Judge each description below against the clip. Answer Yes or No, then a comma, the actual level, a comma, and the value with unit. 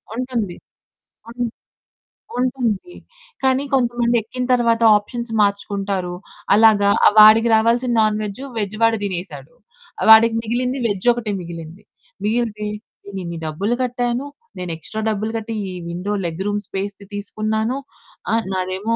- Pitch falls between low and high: No, high, 215 Hz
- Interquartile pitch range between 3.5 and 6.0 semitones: No, average, 3.1 semitones